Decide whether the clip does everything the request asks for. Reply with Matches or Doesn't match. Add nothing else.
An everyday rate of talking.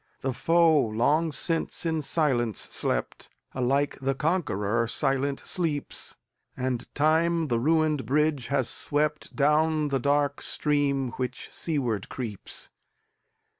Doesn't match